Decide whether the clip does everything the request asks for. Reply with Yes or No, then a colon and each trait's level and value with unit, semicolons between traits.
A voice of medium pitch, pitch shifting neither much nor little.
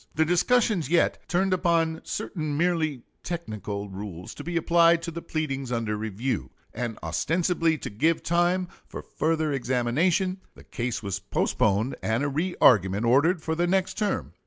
No: medium, 155 Hz; wide, 6.7 semitones